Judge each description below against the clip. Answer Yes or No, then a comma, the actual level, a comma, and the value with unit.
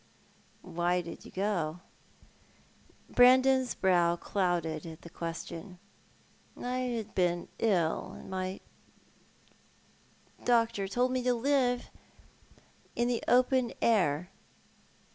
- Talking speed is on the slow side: Yes, slow, 105 wpm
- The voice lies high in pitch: Yes, high, 195 Hz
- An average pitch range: No, wide, 6.0 semitones